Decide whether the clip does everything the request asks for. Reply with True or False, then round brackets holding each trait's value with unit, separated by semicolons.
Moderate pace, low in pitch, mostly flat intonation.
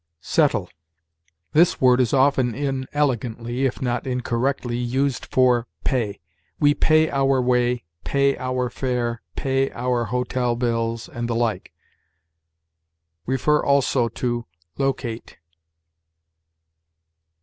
False (100 wpm; 125 Hz; 2.2 semitones)